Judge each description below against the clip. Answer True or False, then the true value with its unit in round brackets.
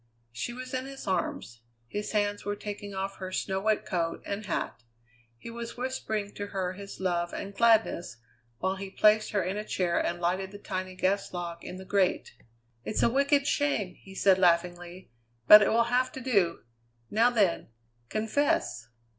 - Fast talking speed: False (180 wpm)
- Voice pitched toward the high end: True (200 Hz)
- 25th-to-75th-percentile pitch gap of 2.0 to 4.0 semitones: True (3.1 semitones)